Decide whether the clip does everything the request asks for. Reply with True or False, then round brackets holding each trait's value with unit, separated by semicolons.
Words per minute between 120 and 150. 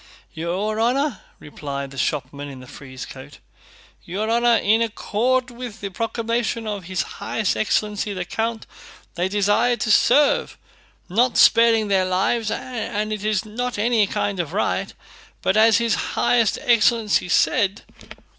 True (145 wpm)